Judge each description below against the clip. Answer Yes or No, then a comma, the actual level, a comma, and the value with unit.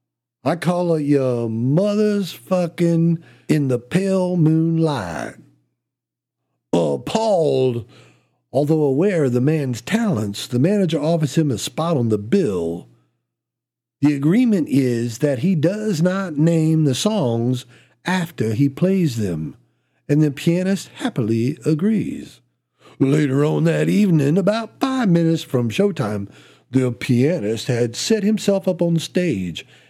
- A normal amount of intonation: No, wide, 6.4 semitones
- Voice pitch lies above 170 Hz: No, medium, 150 Hz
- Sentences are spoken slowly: Yes, slow, 125 wpm